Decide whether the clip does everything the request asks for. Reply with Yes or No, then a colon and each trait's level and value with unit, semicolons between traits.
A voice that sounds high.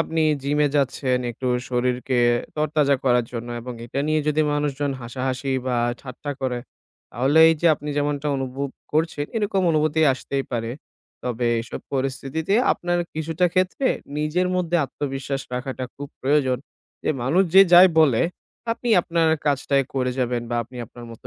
No: medium, 140 Hz